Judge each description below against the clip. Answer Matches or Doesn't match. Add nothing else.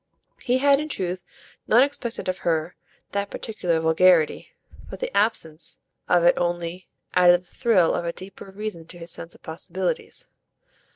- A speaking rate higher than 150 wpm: Matches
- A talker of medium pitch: Matches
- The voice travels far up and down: Doesn't match